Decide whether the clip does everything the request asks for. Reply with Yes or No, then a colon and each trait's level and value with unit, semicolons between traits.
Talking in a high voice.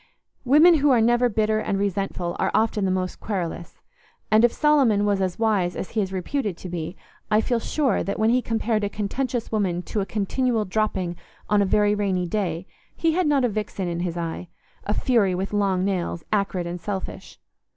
Yes: high, 205 Hz